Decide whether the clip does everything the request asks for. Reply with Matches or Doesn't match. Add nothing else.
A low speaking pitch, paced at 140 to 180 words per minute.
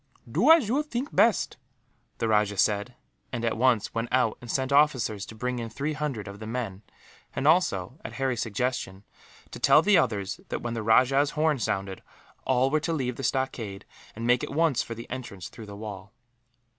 Doesn't match